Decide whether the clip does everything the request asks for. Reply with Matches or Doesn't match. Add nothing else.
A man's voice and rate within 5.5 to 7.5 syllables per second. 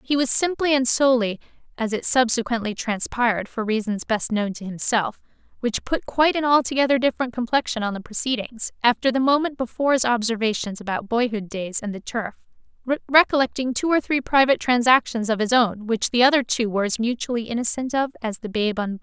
Doesn't match